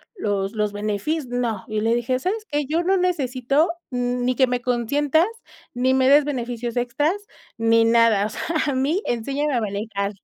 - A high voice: Yes, high, 245 Hz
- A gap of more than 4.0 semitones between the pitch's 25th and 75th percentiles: Yes, average, 4.4 semitones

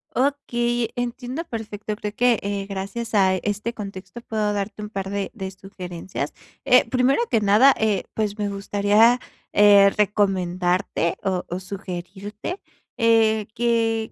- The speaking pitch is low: No, high, 210 Hz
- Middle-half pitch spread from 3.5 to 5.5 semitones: No, average, 2.8 semitones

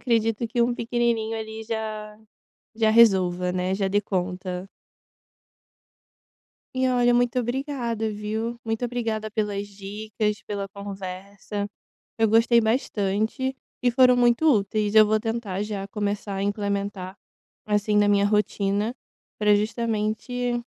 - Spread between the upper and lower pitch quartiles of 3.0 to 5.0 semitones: No, narrow, 2.5 semitones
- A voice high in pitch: Yes, high, 215 Hz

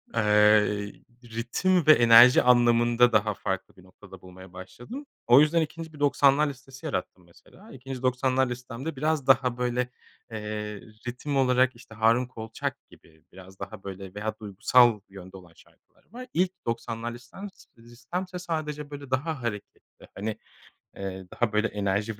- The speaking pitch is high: No, low, 120 Hz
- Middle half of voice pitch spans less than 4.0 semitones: No, average, 4.5 semitones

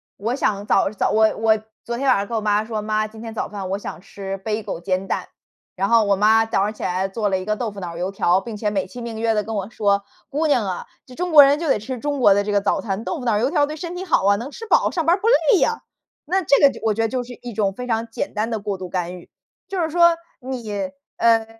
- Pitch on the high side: Yes, high, 220 Hz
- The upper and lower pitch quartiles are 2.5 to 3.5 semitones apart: No, average, 4.2 semitones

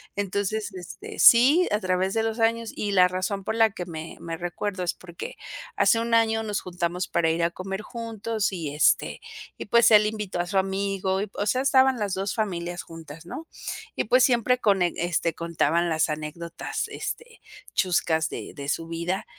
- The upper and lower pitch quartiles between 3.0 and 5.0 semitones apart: Yes, average, 4.4 semitones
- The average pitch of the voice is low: No, high, 190 Hz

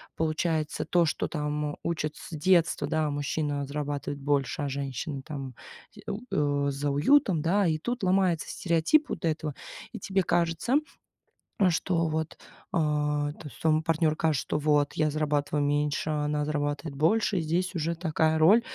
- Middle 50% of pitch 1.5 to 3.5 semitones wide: Yes, narrow, 2.5 semitones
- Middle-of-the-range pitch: Yes, medium, 155 Hz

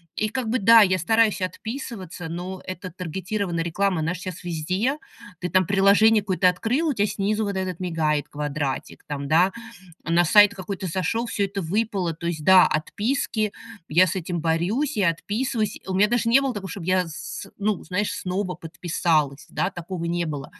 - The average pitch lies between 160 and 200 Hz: Yes, medium, 185 Hz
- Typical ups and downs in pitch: Yes, average, 3.7 semitones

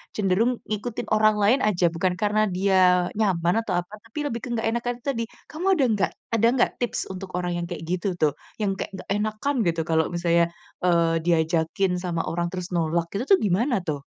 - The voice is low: No, high, 190 Hz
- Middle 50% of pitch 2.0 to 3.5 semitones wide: No, average, 4.0 semitones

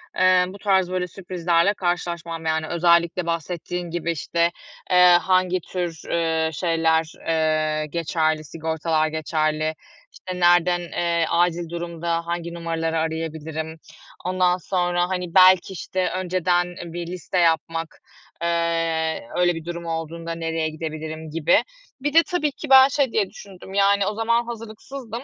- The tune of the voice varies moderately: No, narrow, 2.1 semitones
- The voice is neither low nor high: Yes, medium, 170 Hz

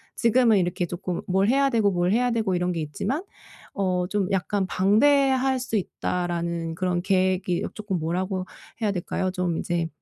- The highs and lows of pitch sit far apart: No, average, 3.6 semitones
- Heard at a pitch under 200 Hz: Yes, medium, 185 Hz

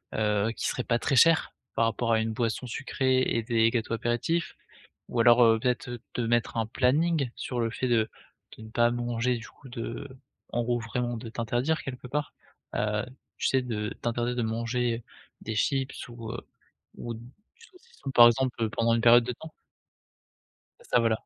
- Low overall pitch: Yes, low, 120 Hz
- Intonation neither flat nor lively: No, narrow, 1.8 semitones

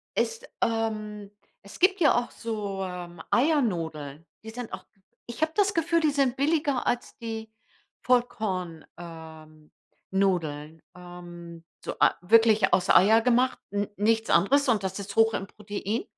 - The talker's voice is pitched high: Yes, high, 210 Hz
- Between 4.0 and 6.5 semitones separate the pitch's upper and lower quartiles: Yes, wide, 5.6 semitones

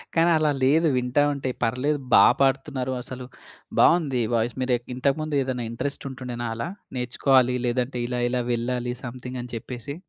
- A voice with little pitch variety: Yes, narrow, 2.0 semitones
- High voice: No, low, 125 Hz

